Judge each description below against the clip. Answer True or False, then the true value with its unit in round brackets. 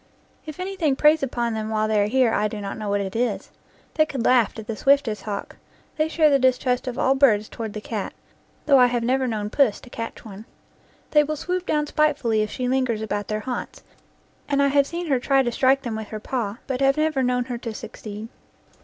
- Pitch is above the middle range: True (250 Hz)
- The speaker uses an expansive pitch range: False (4.2 semitones)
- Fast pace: True (230 wpm)